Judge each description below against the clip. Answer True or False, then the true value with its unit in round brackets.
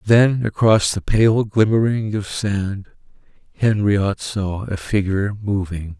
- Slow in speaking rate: True (120 wpm)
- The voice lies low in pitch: True (100 Hz)